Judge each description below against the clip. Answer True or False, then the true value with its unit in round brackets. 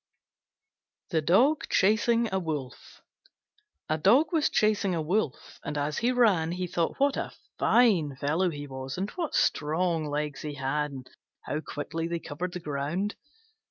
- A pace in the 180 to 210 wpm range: False (160 wpm)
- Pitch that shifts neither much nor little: False (5.7 semitones)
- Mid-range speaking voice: True (165 Hz)